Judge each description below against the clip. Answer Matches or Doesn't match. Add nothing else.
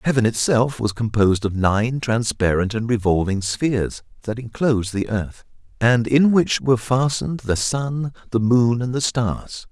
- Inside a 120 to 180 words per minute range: Matches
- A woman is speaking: Doesn't match